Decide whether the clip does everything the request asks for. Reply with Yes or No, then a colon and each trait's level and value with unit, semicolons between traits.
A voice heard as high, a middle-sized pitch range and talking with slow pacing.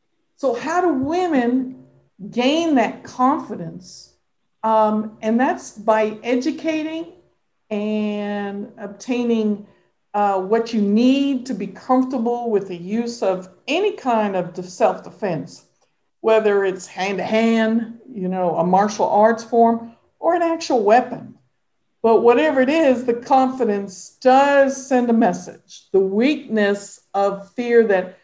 Yes: high, 225 Hz; average, 4.2 semitones; slow, 120 wpm